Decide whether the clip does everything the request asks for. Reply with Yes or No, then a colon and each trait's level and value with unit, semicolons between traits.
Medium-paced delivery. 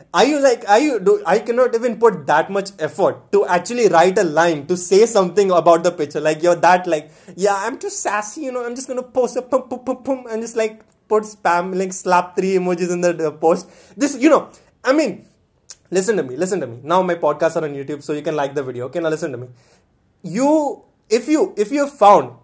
No: fast, 245 wpm